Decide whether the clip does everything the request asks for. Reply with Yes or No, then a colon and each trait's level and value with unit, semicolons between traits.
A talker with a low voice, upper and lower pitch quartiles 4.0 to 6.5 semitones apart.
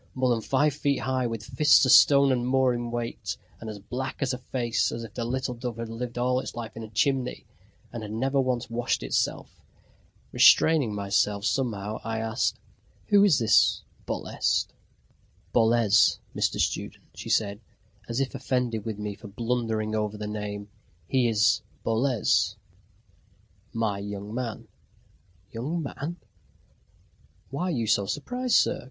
No: low, 120 Hz; average, 3.3 semitones